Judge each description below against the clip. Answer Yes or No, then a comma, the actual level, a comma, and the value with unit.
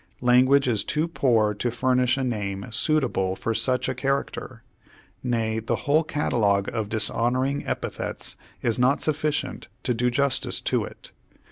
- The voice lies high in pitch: No, low, 125 Hz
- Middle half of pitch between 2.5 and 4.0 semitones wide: Yes, average, 3.7 semitones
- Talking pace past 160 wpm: No, average, 155 wpm